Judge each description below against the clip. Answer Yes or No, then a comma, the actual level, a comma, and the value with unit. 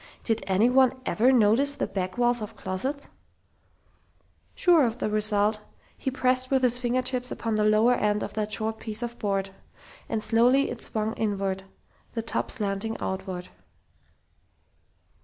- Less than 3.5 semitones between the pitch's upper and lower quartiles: Yes, average, 3.1 semitones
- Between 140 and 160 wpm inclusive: Yes, average, 150 wpm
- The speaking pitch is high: Yes, high, 225 Hz